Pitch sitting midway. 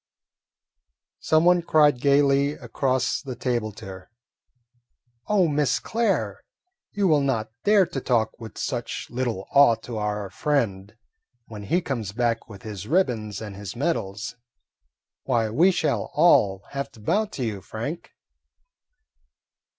No: low, 125 Hz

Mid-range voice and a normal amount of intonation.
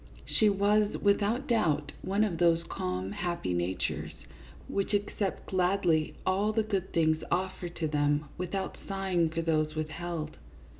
Yes: medium, 175 Hz; average, 4.1 semitones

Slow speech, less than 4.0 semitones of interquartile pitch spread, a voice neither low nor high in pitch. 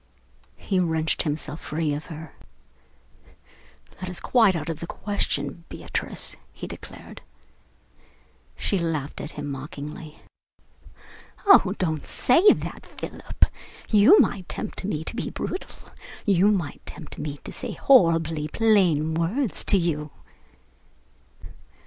No: slow, 120 wpm; average, 4.7 semitones; medium, 165 Hz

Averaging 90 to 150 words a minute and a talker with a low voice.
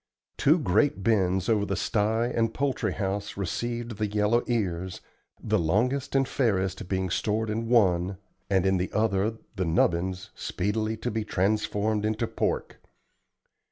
Yes: average, 145 wpm; low, 105 Hz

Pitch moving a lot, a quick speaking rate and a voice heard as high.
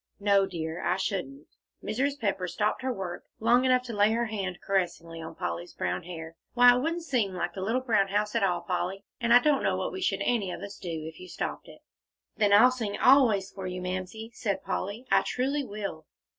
No: average, 4.9 semitones; fast, 215 wpm; high, 200 Hz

